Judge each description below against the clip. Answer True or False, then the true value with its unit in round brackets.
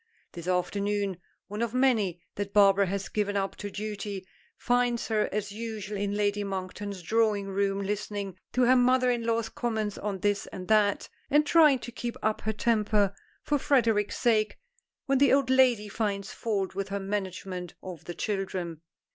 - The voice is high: True (205 Hz)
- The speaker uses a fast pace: False (170 wpm)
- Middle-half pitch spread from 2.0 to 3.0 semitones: True (2.7 semitones)